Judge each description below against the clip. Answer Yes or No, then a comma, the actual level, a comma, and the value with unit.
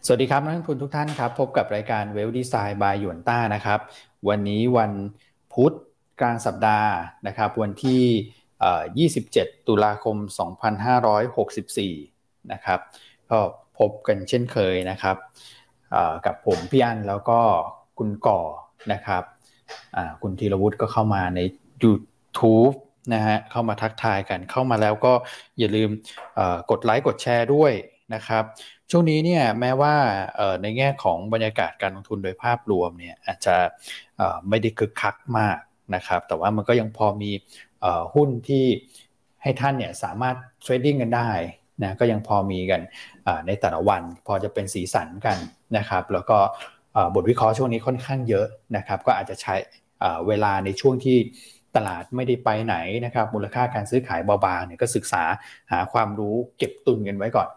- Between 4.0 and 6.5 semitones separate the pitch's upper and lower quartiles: No, average, 3.4 semitones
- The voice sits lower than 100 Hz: No, low, 110 Hz